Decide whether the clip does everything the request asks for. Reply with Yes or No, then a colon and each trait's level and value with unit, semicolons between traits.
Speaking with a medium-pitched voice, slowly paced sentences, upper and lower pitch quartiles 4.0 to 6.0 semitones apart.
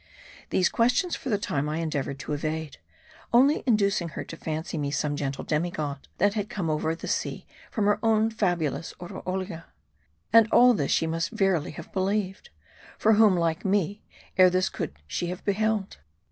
No: medium, 180 Hz; average, 175 wpm; average, 4.7 semitones